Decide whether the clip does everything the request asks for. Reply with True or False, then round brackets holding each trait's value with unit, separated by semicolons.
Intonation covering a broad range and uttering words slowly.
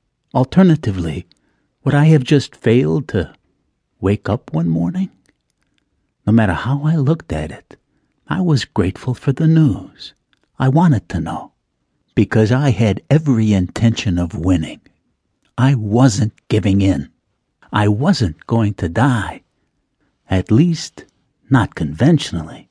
True (6.5 semitones; 125 wpm)